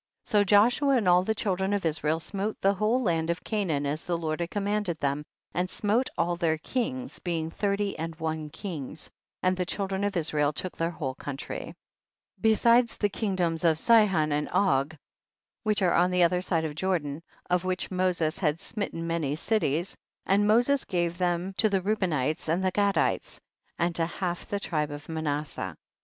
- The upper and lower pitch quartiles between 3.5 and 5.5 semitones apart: Yes, average, 4.2 semitones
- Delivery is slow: No, average, 185 wpm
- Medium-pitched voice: Yes, medium, 180 Hz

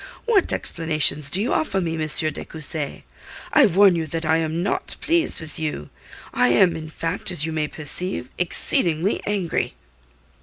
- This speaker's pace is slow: No, average, 165 wpm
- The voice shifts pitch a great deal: No, average, 2.8 semitones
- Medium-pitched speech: Yes, medium, 160 Hz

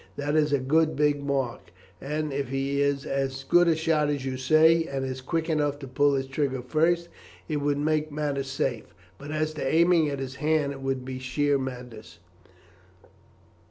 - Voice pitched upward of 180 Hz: No, medium, 140 Hz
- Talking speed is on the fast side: No, average, 190 wpm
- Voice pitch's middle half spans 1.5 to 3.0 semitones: Yes, narrow, 2.4 semitones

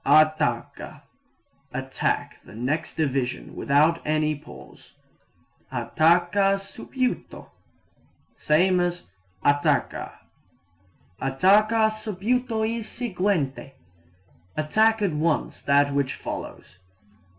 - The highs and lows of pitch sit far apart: Yes, wide, 6.7 semitones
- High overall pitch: No, medium, 170 Hz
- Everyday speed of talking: No, slow, 80 wpm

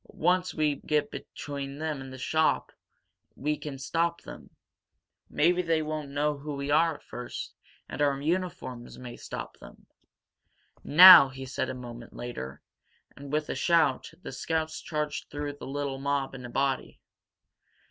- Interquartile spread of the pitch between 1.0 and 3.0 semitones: Yes, average, 2.7 semitones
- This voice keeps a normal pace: Yes, average, 155 wpm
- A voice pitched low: No, medium, 145 Hz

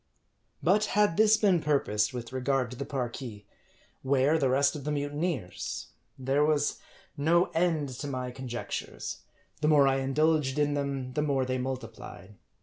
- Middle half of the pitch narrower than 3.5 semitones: Yes, average, 2.9 semitones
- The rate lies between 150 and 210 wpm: Yes, average, 155 wpm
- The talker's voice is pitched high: No, medium, 140 Hz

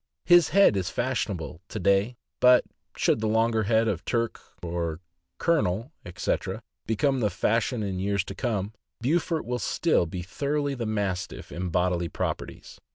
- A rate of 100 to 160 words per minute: Yes, average, 150 wpm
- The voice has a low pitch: Yes, low, 110 Hz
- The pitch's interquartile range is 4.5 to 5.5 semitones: Yes, average, 4.9 semitones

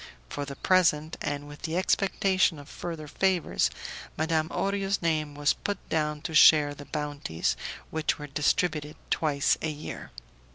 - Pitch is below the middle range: No, medium, 155 Hz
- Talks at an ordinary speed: Yes, average, 150 wpm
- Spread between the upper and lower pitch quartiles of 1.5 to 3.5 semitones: Yes, average, 2.7 semitones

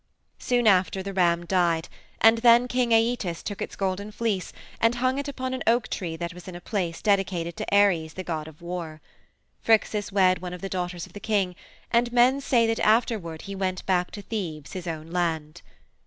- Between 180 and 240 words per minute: Yes, average, 200 wpm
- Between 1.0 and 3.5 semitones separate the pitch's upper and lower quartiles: No, average, 4.6 semitones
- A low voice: No, high, 190 Hz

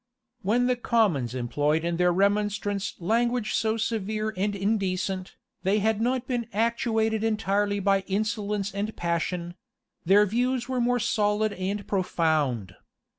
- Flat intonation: No, average, 3.1 semitones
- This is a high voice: Yes, high, 205 Hz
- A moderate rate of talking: No, slow, 130 wpm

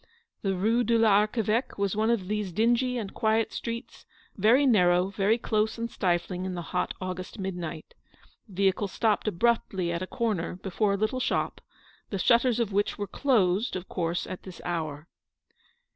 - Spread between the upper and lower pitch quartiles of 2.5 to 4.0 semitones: Yes, average, 3.7 semitones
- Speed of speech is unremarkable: Yes, average, 170 wpm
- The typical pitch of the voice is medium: No, high, 200 Hz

